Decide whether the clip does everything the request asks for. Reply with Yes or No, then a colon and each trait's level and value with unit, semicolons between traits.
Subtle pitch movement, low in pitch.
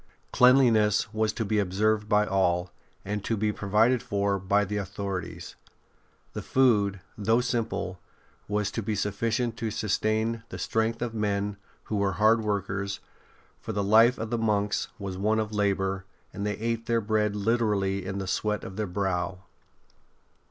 Yes: narrow, 2.1 semitones; low, 105 Hz